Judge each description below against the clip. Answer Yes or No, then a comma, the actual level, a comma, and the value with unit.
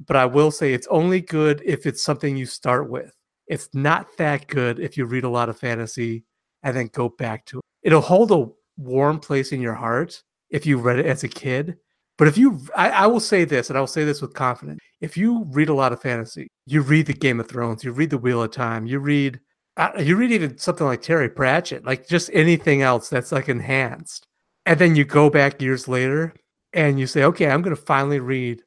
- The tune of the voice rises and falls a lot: No, average, 3.4 semitones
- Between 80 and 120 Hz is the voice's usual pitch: No, medium, 140 Hz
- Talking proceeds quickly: Yes, fast, 230 wpm